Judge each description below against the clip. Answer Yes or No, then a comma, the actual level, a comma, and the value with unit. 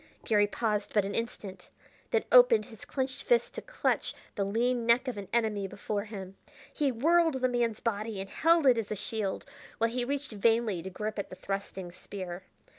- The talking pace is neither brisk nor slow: Yes, average, 190 wpm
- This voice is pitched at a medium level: No, high, 225 Hz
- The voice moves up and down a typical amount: Yes, average, 3.8 semitones